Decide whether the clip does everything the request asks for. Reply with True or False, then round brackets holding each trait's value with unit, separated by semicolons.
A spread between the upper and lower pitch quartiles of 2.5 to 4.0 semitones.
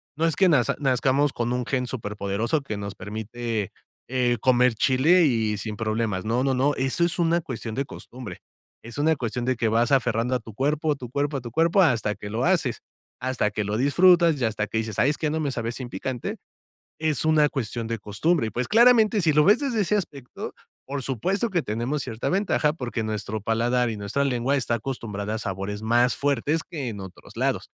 False (5.0 semitones)